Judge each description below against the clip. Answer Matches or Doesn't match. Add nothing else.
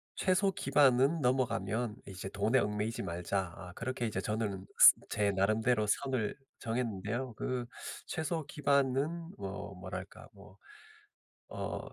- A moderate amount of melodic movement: Matches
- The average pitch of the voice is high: Doesn't match